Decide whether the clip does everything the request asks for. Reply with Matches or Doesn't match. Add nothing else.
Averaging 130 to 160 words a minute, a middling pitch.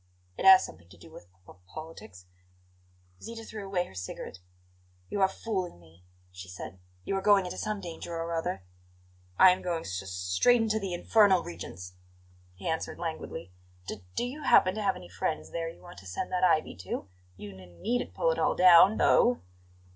Doesn't match